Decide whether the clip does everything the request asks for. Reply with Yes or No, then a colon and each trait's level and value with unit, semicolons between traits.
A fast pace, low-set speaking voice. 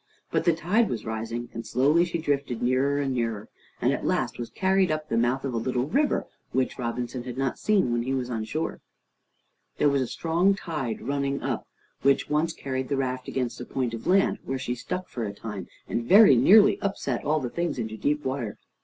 Yes: fast, 215 wpm; low, 130 Hz